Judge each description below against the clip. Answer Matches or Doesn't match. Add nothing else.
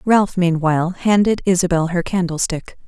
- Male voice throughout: Doesn't match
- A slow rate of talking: Matches